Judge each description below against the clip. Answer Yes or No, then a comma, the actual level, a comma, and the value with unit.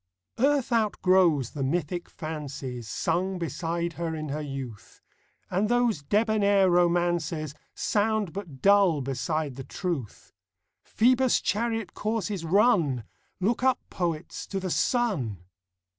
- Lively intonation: Yes, wide, 5.7 semitones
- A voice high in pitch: No, medium, 175 Hz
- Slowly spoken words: Yes, slow, 120 wpm